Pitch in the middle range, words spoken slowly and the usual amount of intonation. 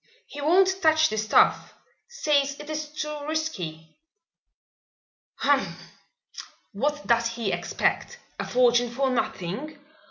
No: very high, 285 Hz; slow, 115 wpm; average, 4.8 semitones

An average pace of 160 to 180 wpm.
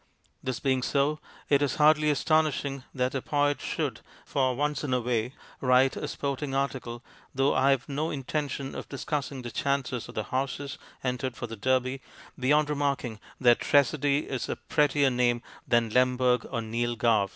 Yes: average, 175 wpm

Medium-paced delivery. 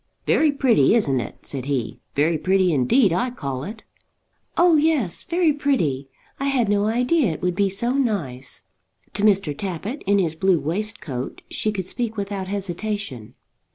Yes: average, 160 wpm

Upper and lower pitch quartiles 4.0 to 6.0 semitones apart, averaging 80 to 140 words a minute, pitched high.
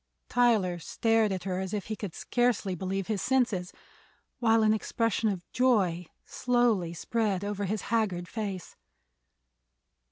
No: average, 3.5 semitones; slow, 135 wpm; high, 205 Hz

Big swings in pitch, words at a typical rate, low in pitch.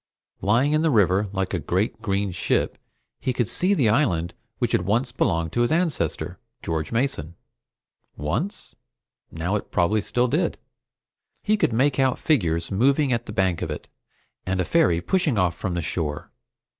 Yes: wide, 7.5 semitones; average, 170 wpm; low, 105 Hz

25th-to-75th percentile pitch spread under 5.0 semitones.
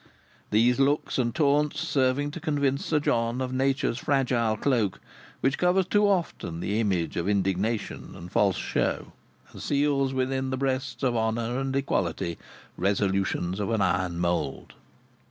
No: wide, 5.4 semitones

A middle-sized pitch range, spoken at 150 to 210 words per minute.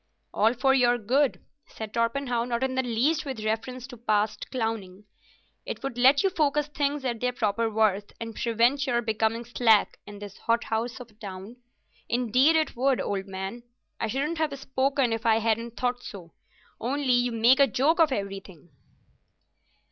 Yes: average, 3.3 semitones; average, 170 wpm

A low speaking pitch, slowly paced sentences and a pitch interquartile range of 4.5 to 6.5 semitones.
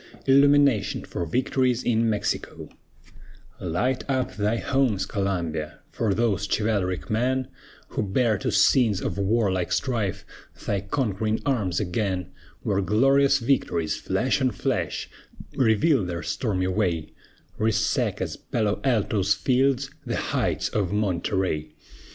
Yes: low, 105 Hz; slow, 115 wpm; average, 5.1 semitones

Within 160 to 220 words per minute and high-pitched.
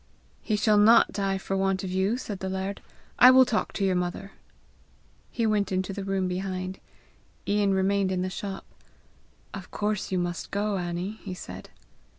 Yes: average, 175 wpm; high, 195 Hz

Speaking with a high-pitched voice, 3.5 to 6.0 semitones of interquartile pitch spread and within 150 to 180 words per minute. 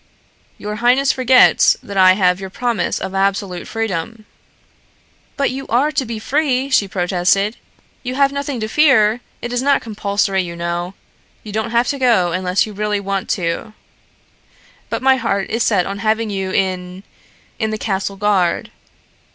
Yes: high, 210 Hz; average, 4.2 semitones; average, 165 wpm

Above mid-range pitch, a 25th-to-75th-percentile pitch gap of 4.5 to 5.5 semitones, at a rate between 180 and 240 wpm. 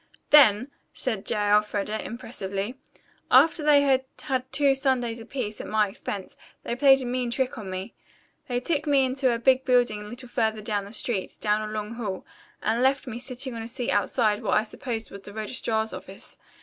No: high, 235 Hz; average, 3.6 semitones; average, 195 wpm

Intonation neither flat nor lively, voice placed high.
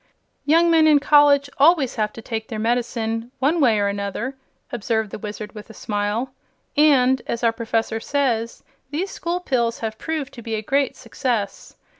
Yes: average, 4.3 semitones; high, 235 Hz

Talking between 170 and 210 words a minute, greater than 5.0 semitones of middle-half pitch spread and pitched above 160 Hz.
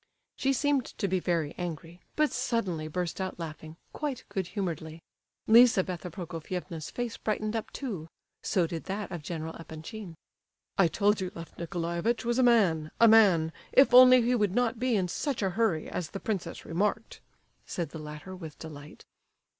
No: average, 160 wpm; wide, 5.4 semitones; medium, 185 Hz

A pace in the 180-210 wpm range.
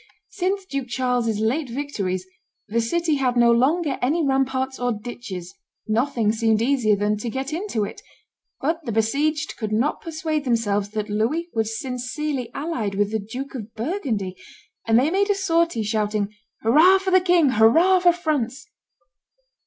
No: average, 160 wpm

